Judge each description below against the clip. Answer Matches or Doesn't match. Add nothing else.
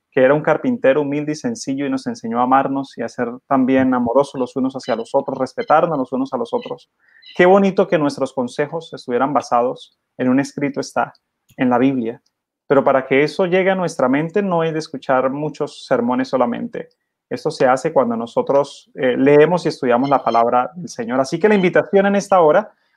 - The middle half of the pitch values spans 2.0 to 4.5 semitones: Doesn't match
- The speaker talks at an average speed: Doesn't match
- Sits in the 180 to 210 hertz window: Doesn't match